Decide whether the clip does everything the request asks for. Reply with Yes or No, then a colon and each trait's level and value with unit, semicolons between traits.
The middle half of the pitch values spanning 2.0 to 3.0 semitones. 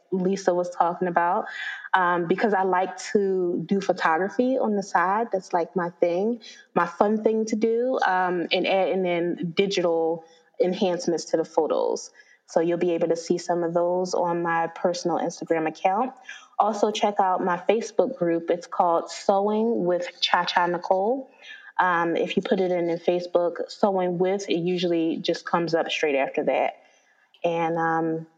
No: average, 3.7 semitones